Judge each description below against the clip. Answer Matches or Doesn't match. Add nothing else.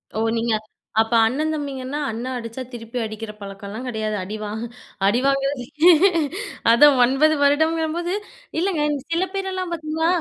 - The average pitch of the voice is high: Matches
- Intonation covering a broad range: Matches